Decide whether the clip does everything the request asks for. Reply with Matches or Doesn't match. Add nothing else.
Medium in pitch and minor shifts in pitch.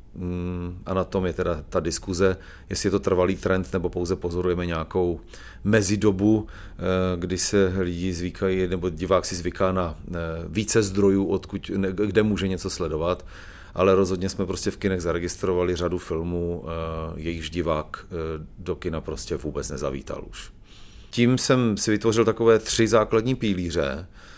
Doesn't match